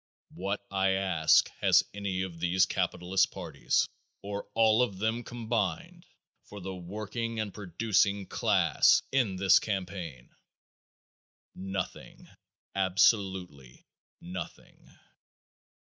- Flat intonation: Yes, narrow, 2.3 semitones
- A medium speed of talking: No, slow, 100 wpm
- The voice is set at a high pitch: No, very low, 95 Hz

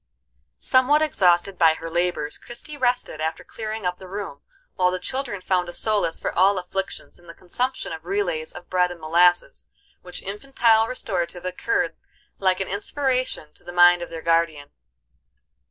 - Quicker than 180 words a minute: No, average, 165 wpm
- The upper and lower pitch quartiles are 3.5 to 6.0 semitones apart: Yes, average, 4.1 semitones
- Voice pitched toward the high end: No, medium, 180 Hz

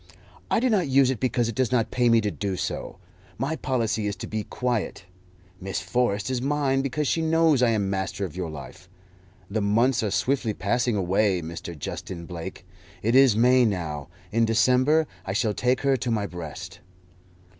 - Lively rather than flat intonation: No, average, 4.9 semitones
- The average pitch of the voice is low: Yes, low, 115 Hz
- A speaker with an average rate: Yes, average, 190 wpm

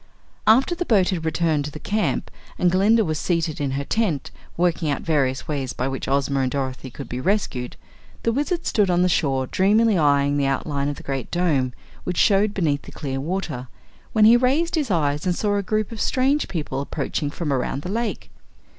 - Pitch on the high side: No, medium, 165 Hz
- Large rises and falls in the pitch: Yes, wide, 6.8 semitones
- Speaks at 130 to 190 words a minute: No, fast, 205 wpm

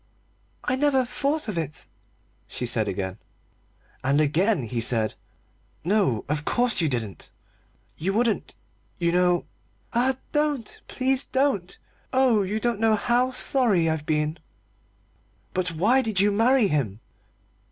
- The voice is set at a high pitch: Yes, high, 195 Hz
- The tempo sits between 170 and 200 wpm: No, average, 140 wpm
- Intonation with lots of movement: Yes, wide, 8.5 semitones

